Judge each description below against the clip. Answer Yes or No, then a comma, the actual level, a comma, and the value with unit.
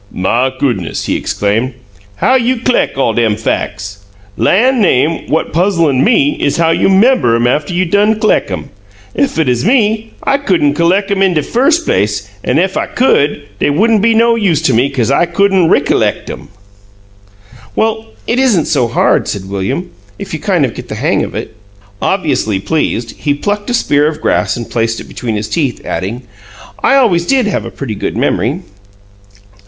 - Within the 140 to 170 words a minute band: No, average, 185 wpm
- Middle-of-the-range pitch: Yes, medium, 165 Hz